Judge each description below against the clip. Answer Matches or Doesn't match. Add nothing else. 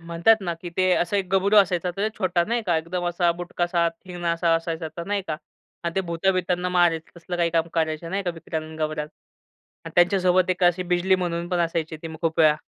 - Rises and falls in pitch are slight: Matches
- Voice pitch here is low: Doesn't match